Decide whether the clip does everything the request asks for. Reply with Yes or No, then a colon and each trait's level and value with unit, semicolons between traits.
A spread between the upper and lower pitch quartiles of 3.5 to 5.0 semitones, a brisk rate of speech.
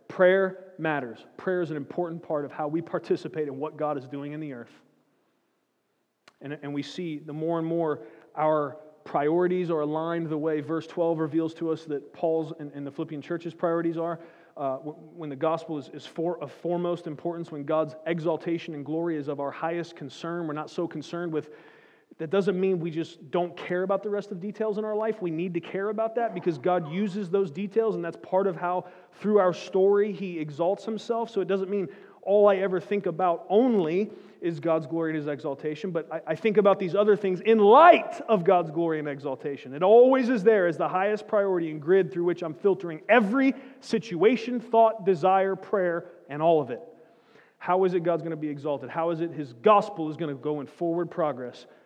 Yes: average, 3.8 semitones; fast, 210 wpm